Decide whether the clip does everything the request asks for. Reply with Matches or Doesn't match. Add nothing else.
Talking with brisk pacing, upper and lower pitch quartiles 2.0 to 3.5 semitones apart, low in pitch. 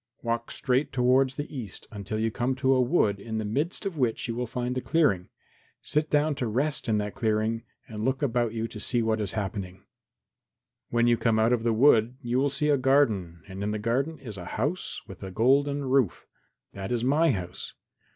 Doesn't match